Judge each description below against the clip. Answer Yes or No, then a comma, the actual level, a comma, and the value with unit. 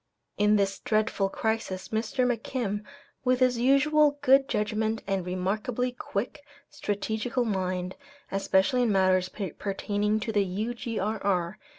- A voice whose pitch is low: No, high, 215 Hz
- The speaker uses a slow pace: Yes, slow, 115 wpm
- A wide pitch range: No, average, 3.9 semitones